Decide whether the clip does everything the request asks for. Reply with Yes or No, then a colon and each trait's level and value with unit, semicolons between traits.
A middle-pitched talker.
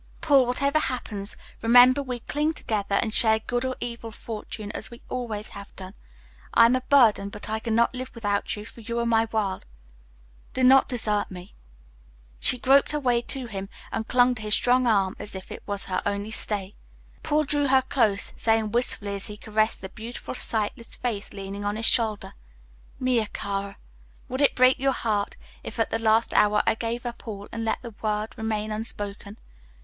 No: high, 225 Hz